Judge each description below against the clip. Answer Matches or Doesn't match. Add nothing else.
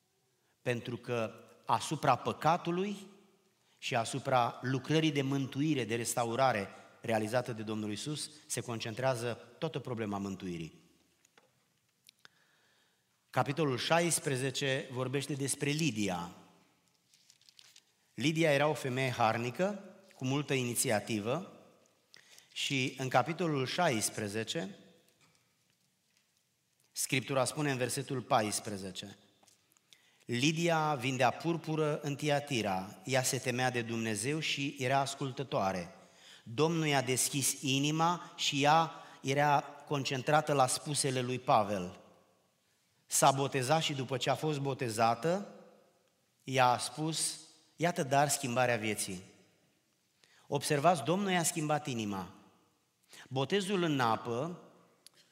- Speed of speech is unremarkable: Doesn't match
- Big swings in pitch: Doesn't match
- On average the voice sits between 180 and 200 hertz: Doesn't match